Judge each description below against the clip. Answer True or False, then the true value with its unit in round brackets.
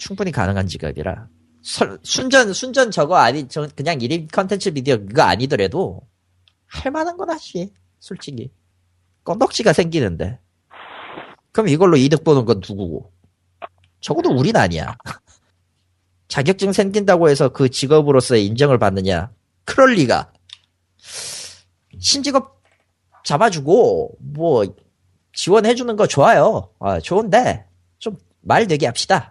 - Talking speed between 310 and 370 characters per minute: False (265 characters per minute)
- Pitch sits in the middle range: False (115 Hz)